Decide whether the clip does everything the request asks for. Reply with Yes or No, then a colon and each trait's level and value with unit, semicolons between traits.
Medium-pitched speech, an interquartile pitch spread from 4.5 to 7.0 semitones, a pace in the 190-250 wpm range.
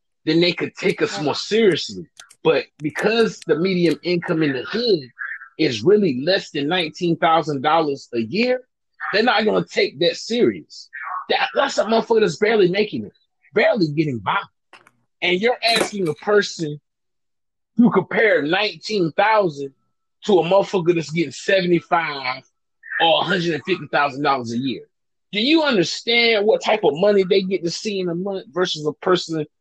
No: medium, 180 Hz; average, 4.9 semitones; average, 150 wpm